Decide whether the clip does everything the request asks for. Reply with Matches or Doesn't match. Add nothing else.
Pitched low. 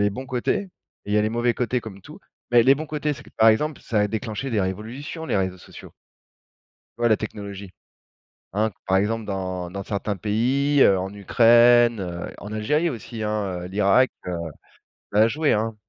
Matches